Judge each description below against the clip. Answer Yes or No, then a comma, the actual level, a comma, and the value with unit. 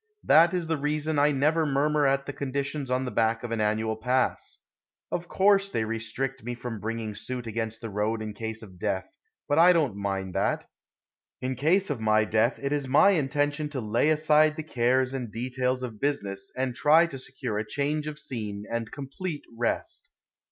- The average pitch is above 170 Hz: No, low, 130 Hz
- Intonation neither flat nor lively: Yes, average, 4.8 semitones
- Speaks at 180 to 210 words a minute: Yes, average, 195 wpm